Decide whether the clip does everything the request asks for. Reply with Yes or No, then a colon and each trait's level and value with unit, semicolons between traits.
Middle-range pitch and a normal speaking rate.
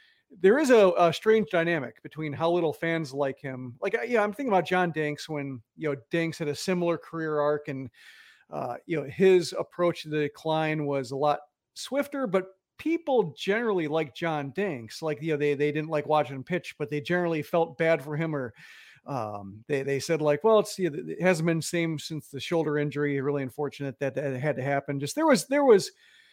No: medium, 155 Hz; fast, 215 wpm